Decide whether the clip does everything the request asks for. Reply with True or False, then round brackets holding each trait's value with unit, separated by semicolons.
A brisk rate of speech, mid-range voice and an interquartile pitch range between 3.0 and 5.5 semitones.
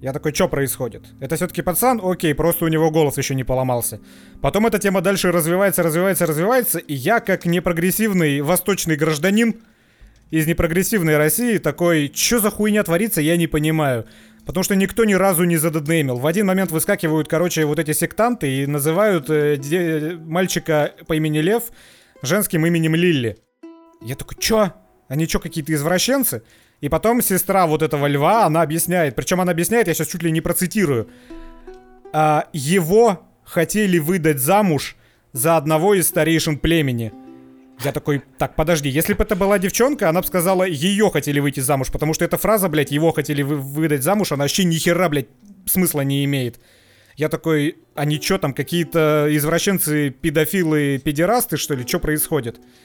True (165 wpm; 160 Hz; 4.1 semitones)